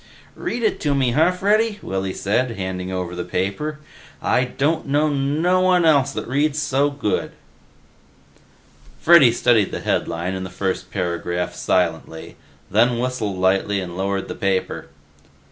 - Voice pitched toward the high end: No, low, 120 Hz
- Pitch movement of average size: No, wide, 8.1 semitones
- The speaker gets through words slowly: No, average, 145 wpm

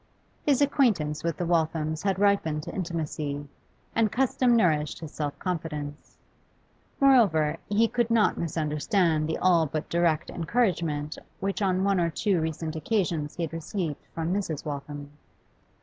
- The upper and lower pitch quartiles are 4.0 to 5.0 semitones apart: Yes, average, 4.6 semitones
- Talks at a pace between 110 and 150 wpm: Yes, average, 145 wpm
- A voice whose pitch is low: No, medium, 165 Hz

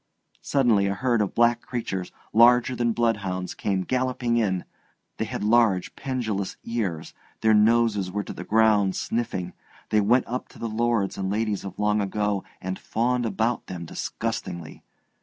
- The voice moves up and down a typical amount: Yes, average, 3.3 semitones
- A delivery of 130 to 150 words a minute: No, average, 160 wpm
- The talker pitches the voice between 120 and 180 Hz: No, low, 110 Hz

